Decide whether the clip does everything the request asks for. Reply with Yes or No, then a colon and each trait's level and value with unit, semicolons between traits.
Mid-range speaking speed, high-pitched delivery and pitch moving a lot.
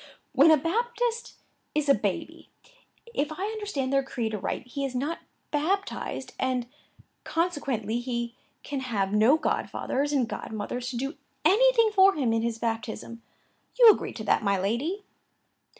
Yes: average, 150 wpm; very high, 270 Hz; wide, 6.3 semitones